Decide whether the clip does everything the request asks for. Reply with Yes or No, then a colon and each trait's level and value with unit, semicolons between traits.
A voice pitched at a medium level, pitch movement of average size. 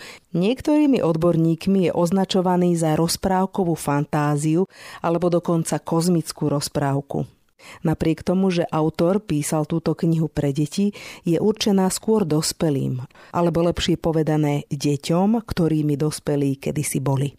Yes: medium, 165 Hz; average, 3.2 semitones